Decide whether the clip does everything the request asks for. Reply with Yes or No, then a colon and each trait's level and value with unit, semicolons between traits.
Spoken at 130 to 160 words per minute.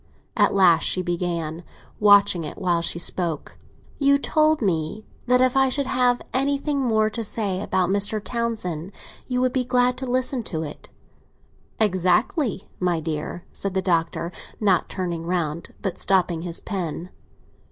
Yes: average, 150 wpm